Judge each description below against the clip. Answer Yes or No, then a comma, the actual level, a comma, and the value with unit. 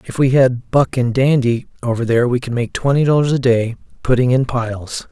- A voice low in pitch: Yes, low, 125 Hz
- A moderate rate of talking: No, fast, 210 wpm